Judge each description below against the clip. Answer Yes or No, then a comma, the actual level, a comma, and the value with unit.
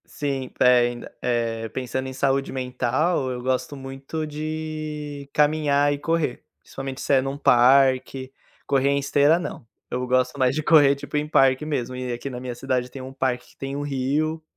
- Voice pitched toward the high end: No, low, 135 Hz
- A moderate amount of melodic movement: No, narrow, 2.3 semitones